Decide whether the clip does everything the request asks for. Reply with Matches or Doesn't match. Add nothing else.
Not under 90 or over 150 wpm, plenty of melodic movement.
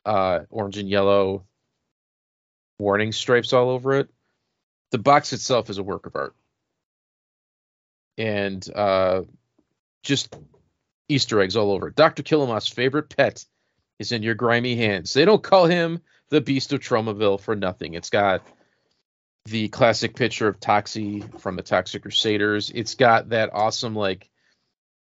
Doesn't match